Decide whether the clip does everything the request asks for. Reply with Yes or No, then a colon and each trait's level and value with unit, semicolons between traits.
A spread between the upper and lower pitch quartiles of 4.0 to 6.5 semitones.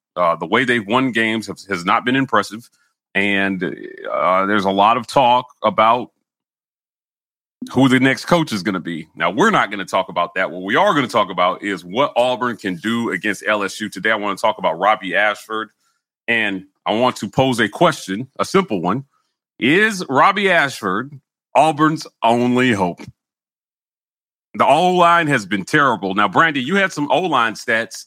Yes: average, 4.6 semitones